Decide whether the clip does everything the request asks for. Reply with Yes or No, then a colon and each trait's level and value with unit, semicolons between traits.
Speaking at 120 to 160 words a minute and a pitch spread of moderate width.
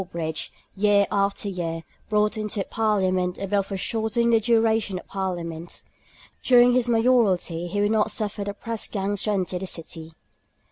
Yes: average, 155 wpm; average, 3.2 semitones